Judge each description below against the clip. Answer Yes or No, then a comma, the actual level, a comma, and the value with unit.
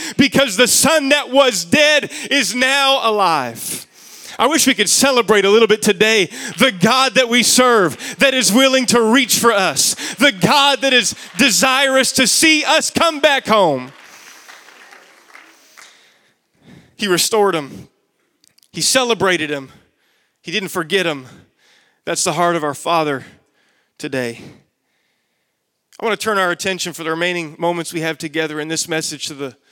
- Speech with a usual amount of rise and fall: No, wide, 7.6 semitones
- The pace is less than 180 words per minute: Yes, average, 155 wpm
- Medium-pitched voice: No, high, 225 Hz